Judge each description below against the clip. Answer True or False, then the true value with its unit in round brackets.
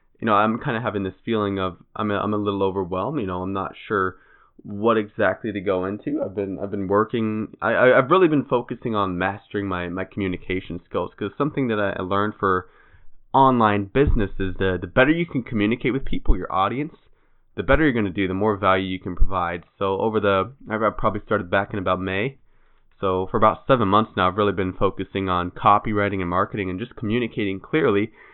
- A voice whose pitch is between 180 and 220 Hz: False (100 Hz)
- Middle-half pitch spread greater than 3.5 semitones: False (2.6 semitones)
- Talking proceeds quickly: True (210 wpm)